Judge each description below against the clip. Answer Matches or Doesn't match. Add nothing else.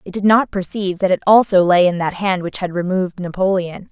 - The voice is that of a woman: Matches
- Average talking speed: Doesn't match